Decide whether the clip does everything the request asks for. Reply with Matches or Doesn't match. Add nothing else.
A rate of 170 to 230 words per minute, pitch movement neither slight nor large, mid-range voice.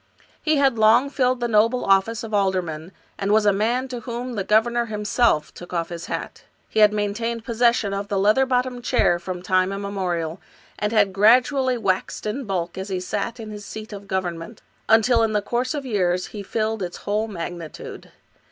Doesn't match